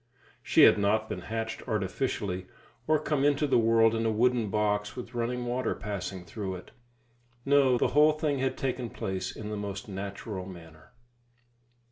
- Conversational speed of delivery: Yes, average, 165 wpm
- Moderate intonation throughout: Yes, average, 4.1 semitones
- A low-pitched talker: Yes, low, 110 Hz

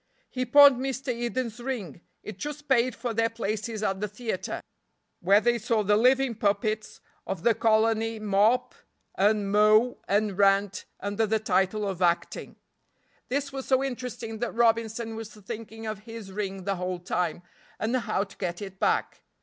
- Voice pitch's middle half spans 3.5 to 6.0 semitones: No, average, 3.0 semitones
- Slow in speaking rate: No, average, 165 wpm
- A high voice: Yes, high, 220 Hz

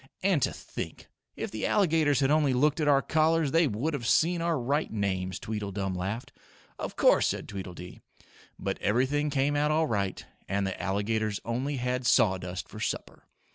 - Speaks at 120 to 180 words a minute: Yes, average, 175 wpm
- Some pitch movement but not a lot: No, wide, 6.8 semitones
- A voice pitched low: Yes, low, 125 Hz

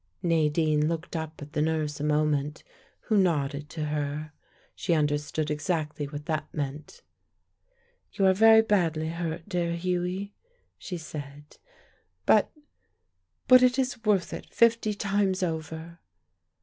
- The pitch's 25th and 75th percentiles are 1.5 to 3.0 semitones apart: No, average, 3.7 semitones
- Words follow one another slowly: Yes, slow, 130 wpm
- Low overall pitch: No, medium, 160 Hz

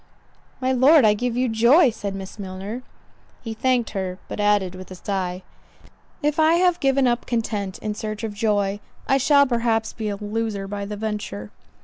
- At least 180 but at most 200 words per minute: Yes, average, 185 wpm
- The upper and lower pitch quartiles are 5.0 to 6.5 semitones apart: No, average, 3.7 semitones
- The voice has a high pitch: Yes, high, 220 Hz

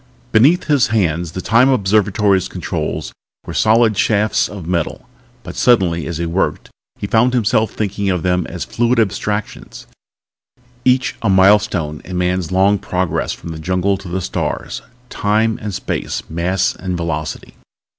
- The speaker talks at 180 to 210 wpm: No, average, 150 wpm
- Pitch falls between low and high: No, very low, 95 Hz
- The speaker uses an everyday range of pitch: Yes, average, 3.5 semitones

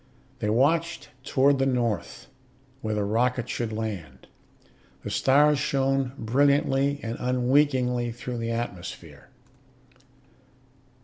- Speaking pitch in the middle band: No, low, 125 Hz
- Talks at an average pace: No, slow, 105 wpm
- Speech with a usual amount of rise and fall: Yes, average, 3.0 semitones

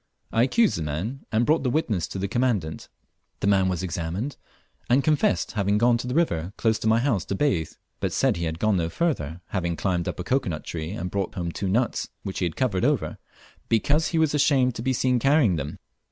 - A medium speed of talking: No, fast, 225 wpm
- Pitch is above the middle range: No, low, 105 Hz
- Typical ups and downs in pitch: No, wide, 6.8 semitones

